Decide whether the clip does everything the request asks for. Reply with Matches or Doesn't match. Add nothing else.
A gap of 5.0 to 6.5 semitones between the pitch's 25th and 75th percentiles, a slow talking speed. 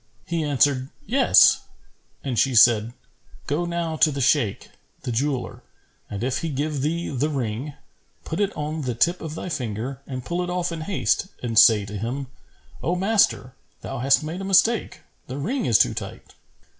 Doesn't match